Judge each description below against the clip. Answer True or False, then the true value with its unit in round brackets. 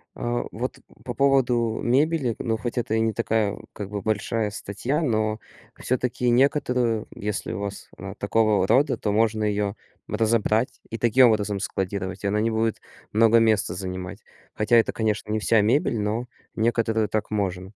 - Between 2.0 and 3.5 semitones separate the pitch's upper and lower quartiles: True (2.4 semitones)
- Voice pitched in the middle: False (110 Hz)